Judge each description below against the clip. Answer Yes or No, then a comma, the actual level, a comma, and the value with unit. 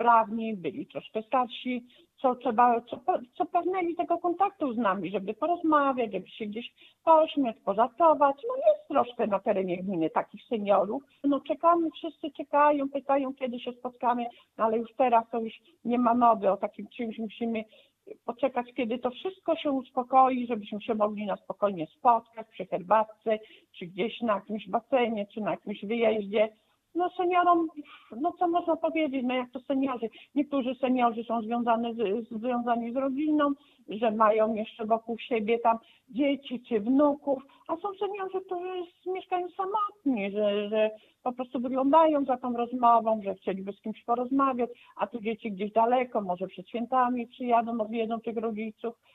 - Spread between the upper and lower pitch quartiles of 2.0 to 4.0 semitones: No, average, 4.4 semitones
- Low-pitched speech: No, high, 240 Hz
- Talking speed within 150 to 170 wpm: Yes, fast, 160 wpm